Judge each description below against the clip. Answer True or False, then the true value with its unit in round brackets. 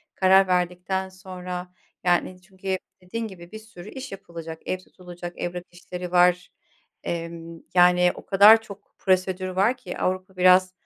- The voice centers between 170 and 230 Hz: True (185 Hz)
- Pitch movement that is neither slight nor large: False (1.2 semitones)